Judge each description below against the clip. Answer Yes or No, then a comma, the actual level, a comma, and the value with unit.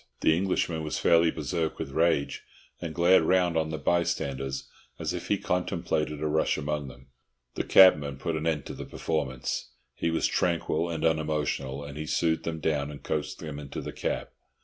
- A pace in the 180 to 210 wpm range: Yes, average, 185 wpm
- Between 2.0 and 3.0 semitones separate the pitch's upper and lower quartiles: Yes, narrow, 2.5 semitones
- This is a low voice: Yes, very low, 80 Hz